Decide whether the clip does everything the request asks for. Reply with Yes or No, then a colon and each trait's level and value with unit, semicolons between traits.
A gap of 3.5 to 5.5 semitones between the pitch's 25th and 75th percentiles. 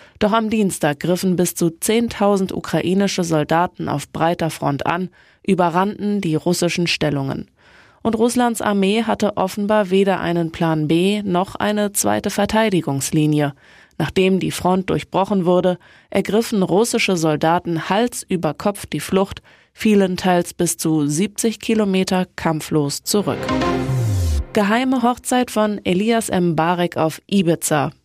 Yes: average, 4.3 semitones